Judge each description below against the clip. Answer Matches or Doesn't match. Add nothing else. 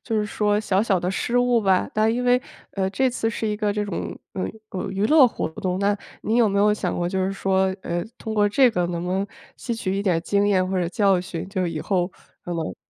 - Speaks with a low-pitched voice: Doesn't match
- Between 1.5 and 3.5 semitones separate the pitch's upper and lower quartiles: Matches